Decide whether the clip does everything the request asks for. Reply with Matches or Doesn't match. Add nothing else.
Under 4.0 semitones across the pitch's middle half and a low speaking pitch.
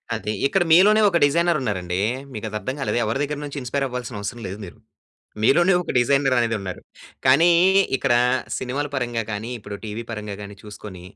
Doesn't match